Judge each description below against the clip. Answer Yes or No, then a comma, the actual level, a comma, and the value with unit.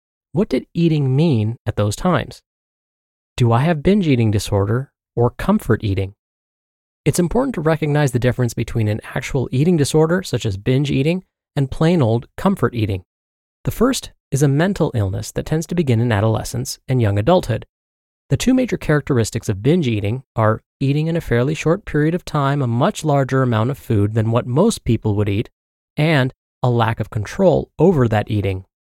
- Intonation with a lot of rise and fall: Yes, wide, 6.0 semitones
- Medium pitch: No, low, 125 Hz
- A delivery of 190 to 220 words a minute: No, average, 180 wpm